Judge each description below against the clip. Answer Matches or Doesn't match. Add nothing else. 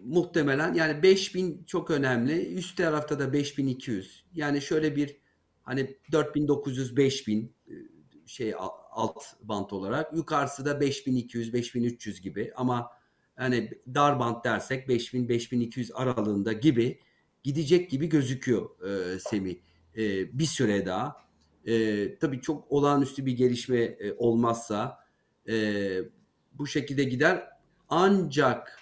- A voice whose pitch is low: Matches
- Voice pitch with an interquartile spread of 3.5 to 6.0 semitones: Matches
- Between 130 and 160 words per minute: Doesn't match